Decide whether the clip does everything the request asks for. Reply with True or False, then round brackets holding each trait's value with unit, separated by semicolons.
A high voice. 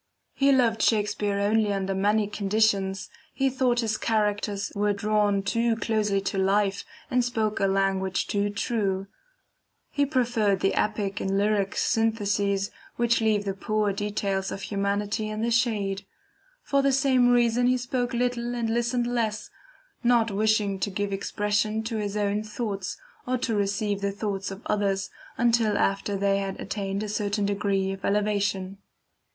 True (210 Hz)